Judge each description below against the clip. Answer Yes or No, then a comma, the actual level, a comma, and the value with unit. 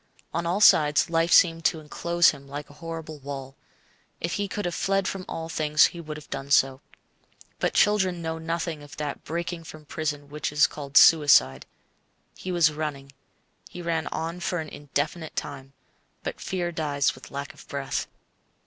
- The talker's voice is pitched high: No, medium, 155 Hz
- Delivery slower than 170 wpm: No, average, 175 wpm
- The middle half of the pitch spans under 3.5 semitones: Yes, average, 2.9 semitones